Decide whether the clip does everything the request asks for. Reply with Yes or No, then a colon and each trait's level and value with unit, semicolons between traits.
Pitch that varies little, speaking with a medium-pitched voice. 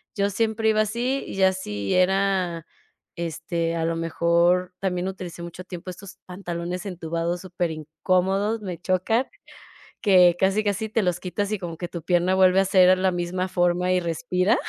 Yes: narrow, 2.2 semitones; medium, 180 Hz